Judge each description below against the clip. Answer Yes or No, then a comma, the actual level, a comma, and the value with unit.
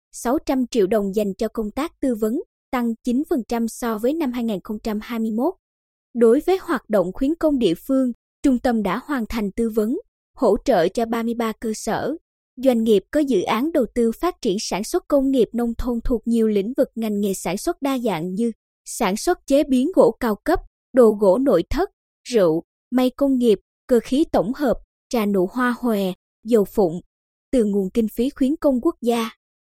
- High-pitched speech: Yes, high, 240 Hz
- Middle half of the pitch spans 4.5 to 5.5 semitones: No, average, 3.8 semitones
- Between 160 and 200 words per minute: Yes, average, 190 wpm